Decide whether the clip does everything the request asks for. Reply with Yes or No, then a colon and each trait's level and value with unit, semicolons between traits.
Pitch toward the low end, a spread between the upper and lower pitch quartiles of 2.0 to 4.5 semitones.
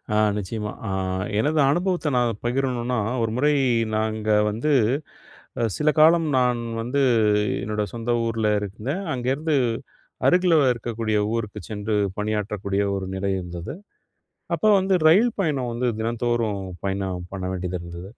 No: low, 115 Hz; average, 5.0 semitones